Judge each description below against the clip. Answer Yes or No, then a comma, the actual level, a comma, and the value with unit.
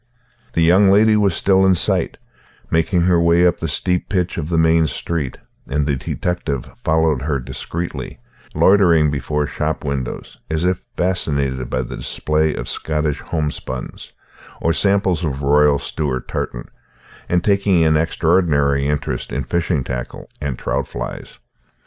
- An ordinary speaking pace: Yes, average, 150 wpm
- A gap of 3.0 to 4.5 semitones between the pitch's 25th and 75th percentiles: Yes, average, 3.6 semitones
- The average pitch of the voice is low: Yes, very low, 80 Hz